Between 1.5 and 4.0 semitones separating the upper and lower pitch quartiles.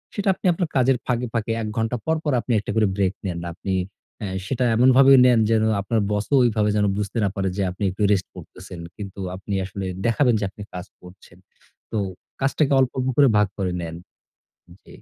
No: average, 4.6 semitones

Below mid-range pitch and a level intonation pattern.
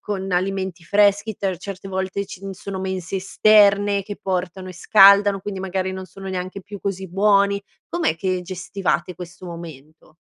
No: high, 190 Hz; narrow, 1.5 semitones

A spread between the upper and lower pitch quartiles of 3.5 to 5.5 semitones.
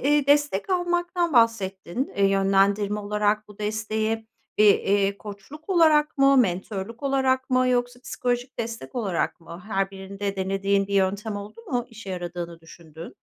Yes: average, 4.6 semitones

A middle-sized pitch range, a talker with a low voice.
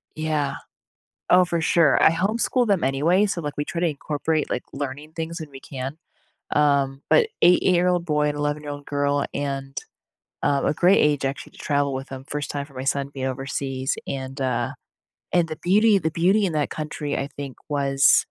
No: average, 3.4 semitones; medium, 145 Hz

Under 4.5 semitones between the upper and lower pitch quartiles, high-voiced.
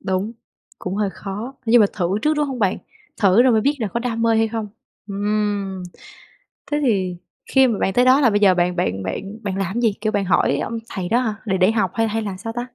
Yes: average, 3.2 semitones; high, 210 Hz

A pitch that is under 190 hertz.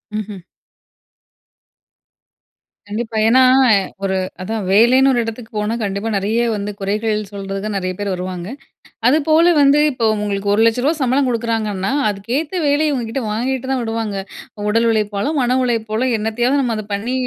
No: high, 225 Hz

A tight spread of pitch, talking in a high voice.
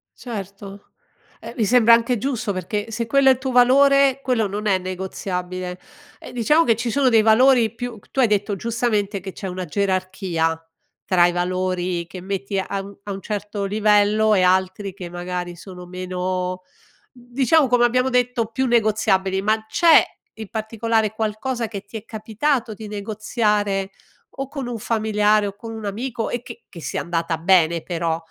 No: average, 3.8 semitones; high, 210 Hz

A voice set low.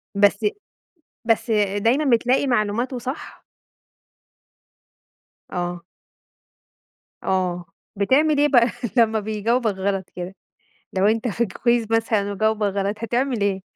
No: high, 220 Hz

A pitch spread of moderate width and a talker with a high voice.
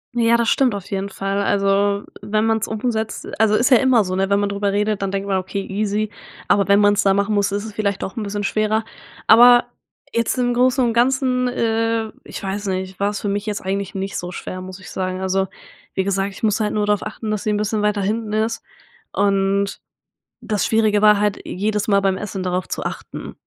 No: narrow, 2.0 semitones; high, 205 Hz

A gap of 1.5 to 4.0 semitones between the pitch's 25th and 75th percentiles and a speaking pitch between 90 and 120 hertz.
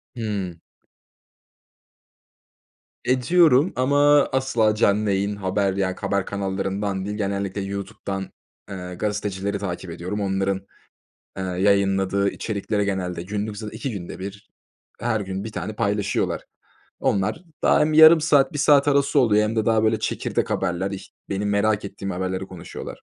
Yes: narrow, 2.4 semitones; low, 100 Hz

